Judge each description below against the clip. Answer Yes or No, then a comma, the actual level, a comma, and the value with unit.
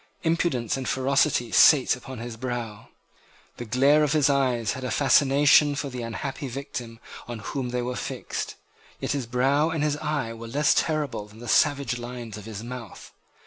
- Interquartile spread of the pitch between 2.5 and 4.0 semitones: Yes, average, 3.3 semitones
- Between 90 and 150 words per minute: No, average, 180 wpm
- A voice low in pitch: Yes, low, 125 Hz